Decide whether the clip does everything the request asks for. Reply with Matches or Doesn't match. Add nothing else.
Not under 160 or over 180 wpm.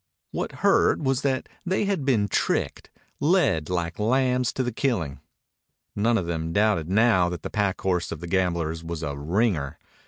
Matches